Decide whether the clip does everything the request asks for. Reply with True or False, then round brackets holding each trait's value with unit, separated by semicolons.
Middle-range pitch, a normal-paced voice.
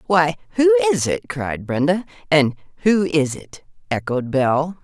True (170 Hz; 150 wpm)